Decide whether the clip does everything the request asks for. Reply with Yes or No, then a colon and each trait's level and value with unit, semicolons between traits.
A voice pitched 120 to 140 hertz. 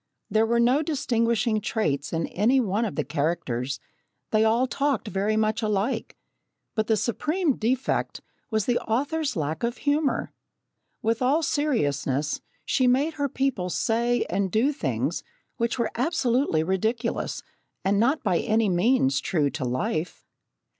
No: high, 225 Hz